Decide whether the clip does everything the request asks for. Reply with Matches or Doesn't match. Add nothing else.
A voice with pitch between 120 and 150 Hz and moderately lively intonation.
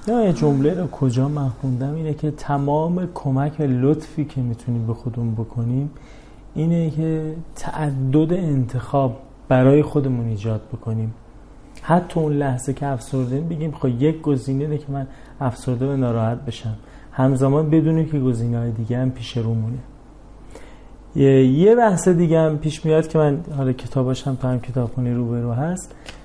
Matches